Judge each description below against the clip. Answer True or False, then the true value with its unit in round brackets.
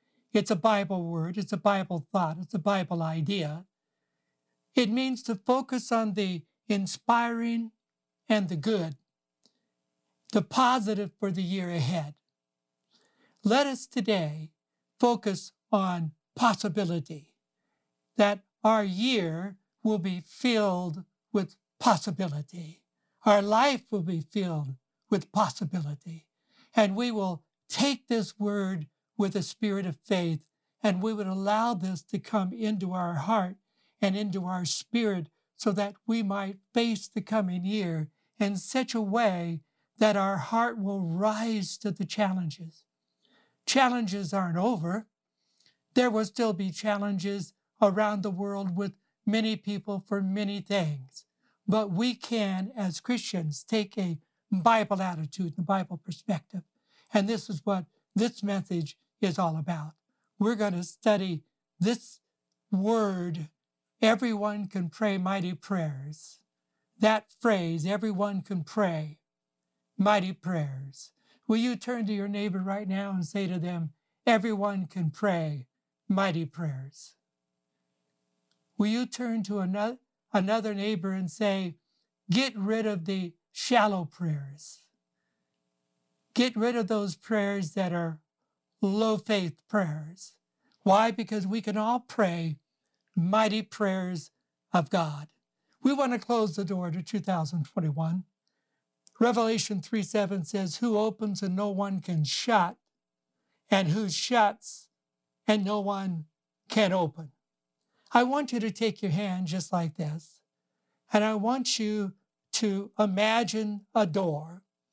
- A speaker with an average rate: False (130 wpm)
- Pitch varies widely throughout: False (4.3 semitones)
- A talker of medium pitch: False (195 Hz)